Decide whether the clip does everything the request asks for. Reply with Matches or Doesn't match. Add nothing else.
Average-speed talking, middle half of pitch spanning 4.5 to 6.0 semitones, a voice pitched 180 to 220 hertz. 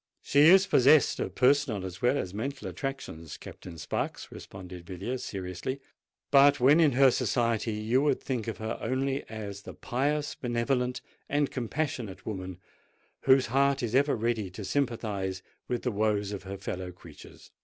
Doesn't match